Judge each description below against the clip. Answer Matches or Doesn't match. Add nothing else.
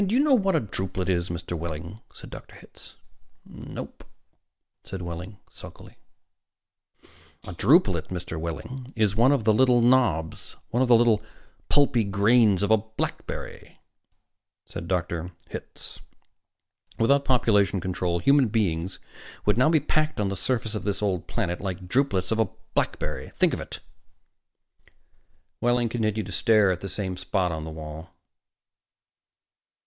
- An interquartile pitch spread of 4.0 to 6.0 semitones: Matches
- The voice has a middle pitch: Doesn't match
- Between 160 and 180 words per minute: Doesn't match